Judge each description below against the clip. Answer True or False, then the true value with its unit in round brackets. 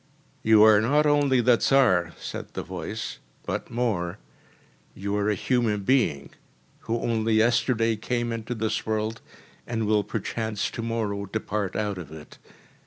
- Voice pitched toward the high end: False (110 Hz)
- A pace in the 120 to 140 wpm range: False (150 wpm)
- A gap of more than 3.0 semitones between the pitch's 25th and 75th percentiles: False (2.5 semitones)